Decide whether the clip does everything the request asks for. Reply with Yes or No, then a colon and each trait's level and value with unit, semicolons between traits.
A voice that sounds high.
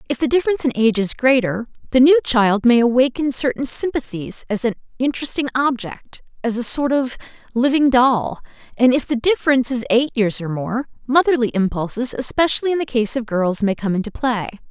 Yes: high, 245 Hz